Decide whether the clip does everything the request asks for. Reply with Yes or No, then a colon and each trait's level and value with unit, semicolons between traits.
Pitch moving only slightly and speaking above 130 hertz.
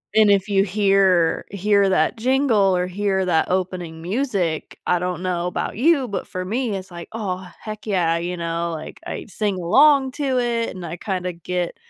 No: average, 3.2 semitones; high, 190 Hz